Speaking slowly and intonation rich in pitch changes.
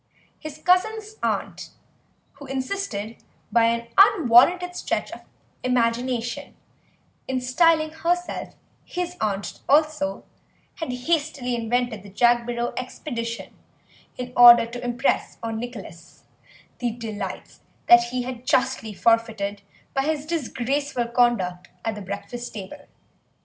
No: slow, 115 wpm; average, 3.9 semitones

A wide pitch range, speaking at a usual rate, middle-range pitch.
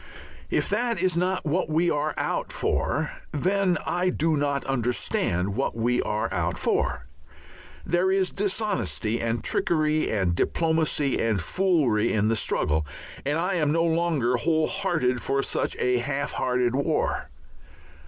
Yes: wide, 6.4 semitones; average, 145 wpm; medium, 145 Hz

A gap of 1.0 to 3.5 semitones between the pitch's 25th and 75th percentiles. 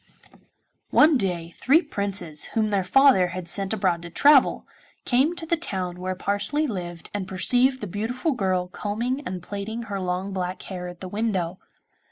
No: average, 5.3 semitones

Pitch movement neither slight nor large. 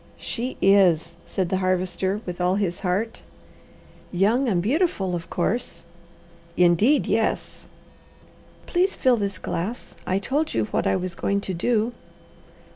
Yes: average, 4.5 semitones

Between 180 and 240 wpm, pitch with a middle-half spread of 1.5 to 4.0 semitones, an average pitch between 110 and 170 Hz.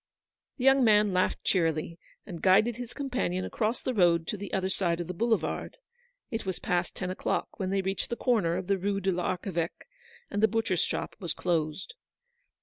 No: average, 195 wpm; average, 3.7 semitones; high, 190 Hz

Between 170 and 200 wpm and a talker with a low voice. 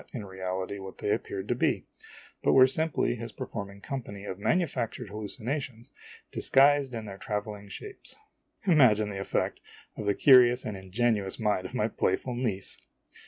No: average, 155 wpm; low, 110 Hz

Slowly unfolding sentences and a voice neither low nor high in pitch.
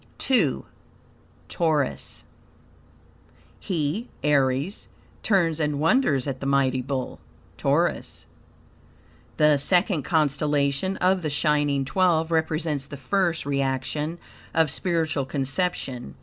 Yes: slow, 95 wpm; medium, 150 Hz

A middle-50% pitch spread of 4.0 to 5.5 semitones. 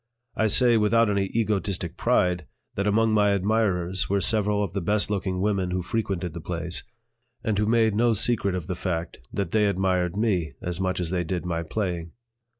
No: average, 2.9 semitones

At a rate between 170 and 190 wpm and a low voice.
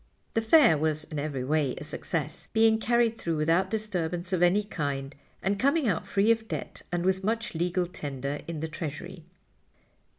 No: average, 175 wpm; medium, 175 Hz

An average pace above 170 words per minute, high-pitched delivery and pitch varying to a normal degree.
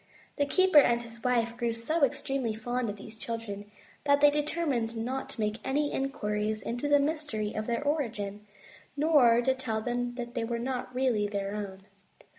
Yes: average, 180 wpm; high, 240 Hz; average, 4.0 semitones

